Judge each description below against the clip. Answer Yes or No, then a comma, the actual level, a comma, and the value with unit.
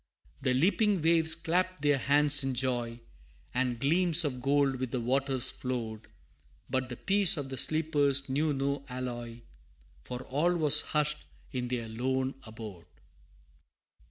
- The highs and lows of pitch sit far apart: No, average, 3.3 semitones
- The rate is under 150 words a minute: Yes, average, 140 wpm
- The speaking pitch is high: No, low, 135 Hz